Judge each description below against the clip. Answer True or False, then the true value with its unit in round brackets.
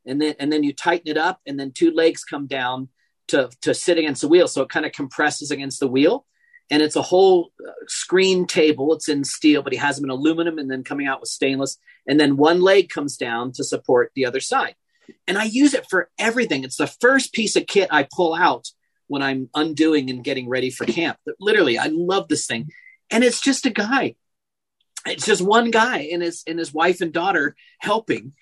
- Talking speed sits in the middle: False (225 wpm)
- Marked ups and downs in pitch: True (7.0 semitones)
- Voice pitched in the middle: True (160 Hz)